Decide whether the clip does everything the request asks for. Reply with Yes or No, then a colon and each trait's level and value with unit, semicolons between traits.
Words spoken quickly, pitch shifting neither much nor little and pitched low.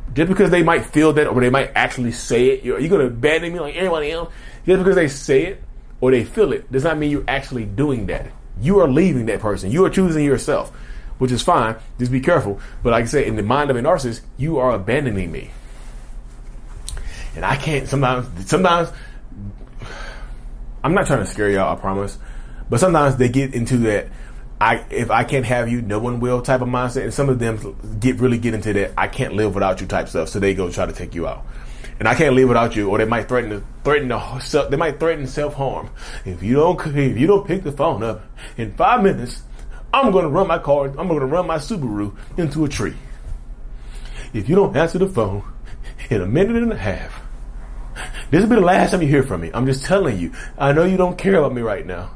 No: fast, 230 wpm; wide, 6.0 semitones; low, 130 Hz